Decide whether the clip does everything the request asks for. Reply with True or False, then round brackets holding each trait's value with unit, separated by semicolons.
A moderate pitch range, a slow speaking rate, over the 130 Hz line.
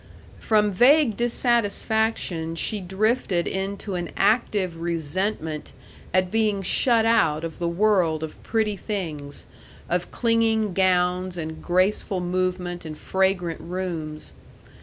True (3.9 semitones; 115 wpm; 185 Hz)